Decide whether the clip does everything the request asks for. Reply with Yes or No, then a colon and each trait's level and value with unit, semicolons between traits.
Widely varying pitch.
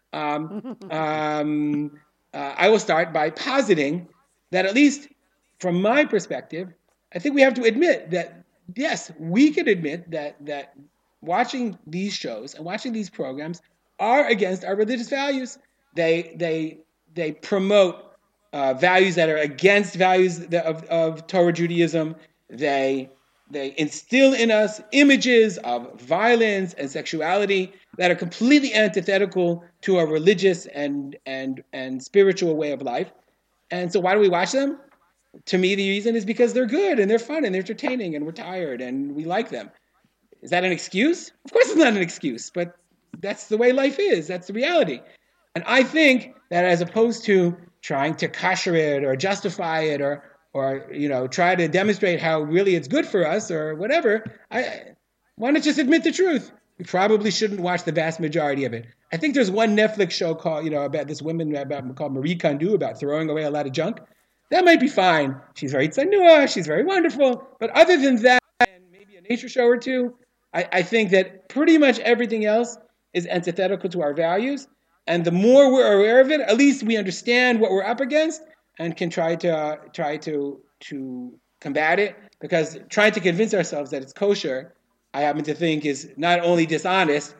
Yes: wide, 6.9 semitones